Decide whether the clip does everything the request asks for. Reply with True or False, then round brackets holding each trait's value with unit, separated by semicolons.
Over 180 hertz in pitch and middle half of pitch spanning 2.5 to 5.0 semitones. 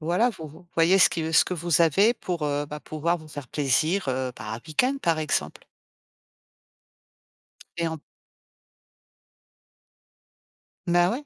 False (165 Hz; 2.9 semitones)